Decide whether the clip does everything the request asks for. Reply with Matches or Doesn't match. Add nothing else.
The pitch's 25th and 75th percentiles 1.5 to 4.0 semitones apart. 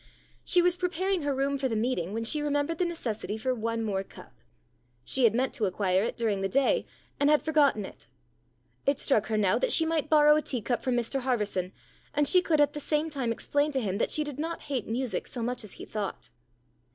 Doesn't match